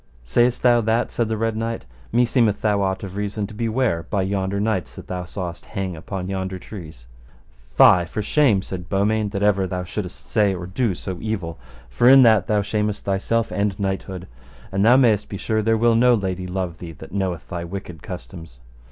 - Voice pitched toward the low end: Yes, low, 100 Hz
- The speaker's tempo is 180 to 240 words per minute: Yes, average, 200 wpm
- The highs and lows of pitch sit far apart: No, average, 3.2 semitones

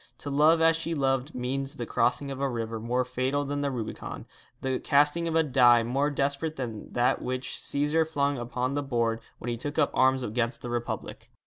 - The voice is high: No, low, 135 Hz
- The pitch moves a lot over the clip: No, average, 2.8 semitones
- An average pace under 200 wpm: No, fast, 205 wpm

